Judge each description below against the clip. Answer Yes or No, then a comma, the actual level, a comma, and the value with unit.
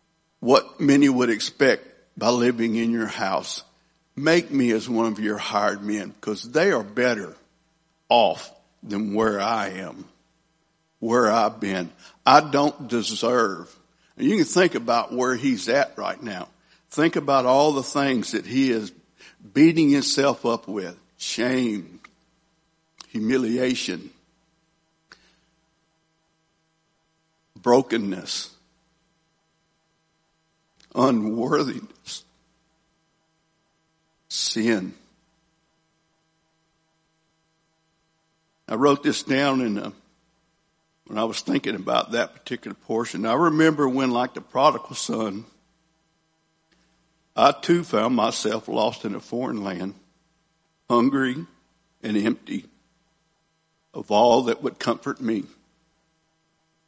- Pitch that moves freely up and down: No, average, 4.4 semitones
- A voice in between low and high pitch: Yes, medium, 160 Hz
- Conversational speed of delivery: No, slow, 105 wpm